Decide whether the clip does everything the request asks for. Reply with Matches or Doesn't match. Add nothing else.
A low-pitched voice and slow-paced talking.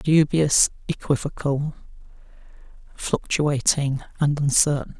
Doesn't match